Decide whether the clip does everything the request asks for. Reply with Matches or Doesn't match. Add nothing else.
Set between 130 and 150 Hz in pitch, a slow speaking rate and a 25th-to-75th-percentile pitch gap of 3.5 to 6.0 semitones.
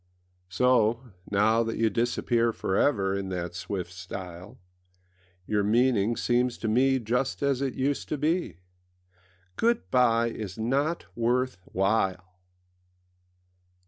Doesn't match